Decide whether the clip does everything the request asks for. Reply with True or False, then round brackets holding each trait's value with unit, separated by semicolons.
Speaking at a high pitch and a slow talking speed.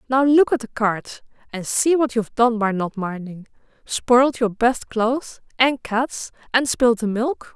False (235 Hz; 185 wpm)